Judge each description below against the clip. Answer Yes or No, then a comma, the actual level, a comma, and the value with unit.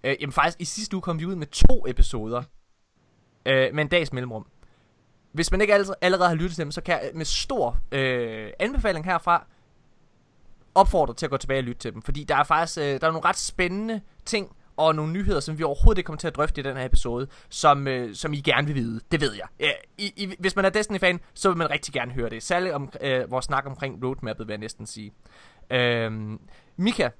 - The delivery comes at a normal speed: No, fast, 235 wpm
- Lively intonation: Yes, wide, 6.1 semitones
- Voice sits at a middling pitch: Yes, medium, 145 Hz